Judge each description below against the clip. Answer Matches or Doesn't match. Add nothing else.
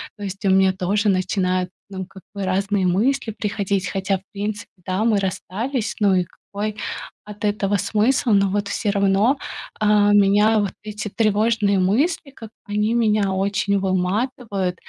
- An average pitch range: Doesn't match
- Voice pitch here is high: Matches